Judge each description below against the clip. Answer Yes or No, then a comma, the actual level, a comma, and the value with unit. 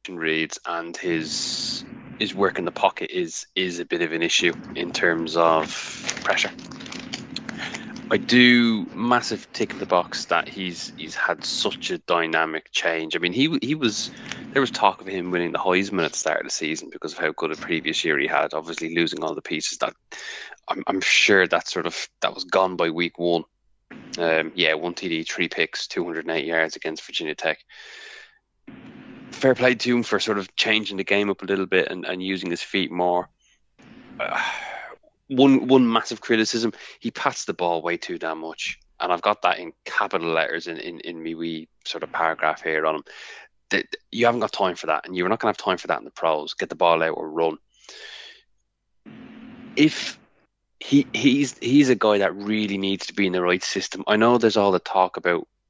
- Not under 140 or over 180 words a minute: No, fast, 205 wpm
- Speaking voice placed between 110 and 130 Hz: No, low, 100 Hz